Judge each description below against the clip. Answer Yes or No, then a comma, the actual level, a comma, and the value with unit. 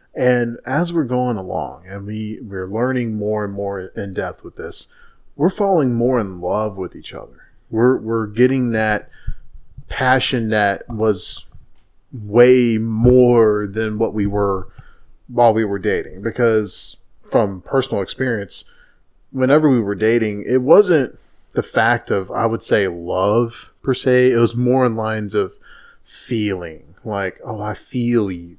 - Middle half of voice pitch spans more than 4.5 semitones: No, average, 3.2 semitones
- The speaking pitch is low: Yes, low, 115 Hz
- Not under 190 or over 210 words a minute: No, average, 150 wpm